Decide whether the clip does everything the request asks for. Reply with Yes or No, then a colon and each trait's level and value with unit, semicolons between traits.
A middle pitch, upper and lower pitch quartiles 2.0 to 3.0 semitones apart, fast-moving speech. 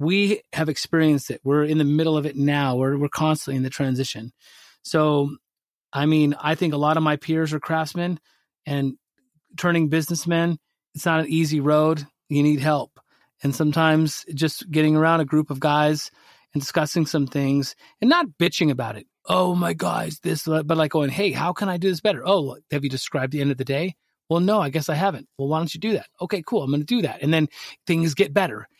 Yes: medium, 155 Hz; narrow, 2.6 semitones; fast, 220 wpm